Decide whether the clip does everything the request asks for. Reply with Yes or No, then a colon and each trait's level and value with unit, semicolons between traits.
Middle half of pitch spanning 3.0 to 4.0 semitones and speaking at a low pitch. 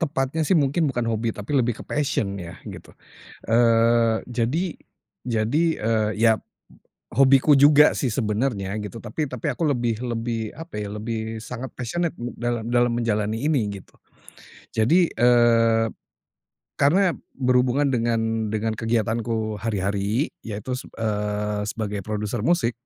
Yes: average, 3.3 semitones; low, 115 Hz